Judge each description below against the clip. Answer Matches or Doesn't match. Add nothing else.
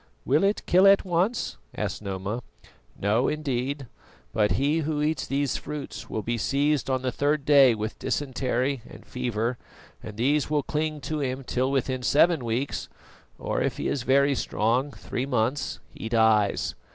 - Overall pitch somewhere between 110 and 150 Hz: Matches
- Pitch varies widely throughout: Doesn't match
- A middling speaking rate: Matches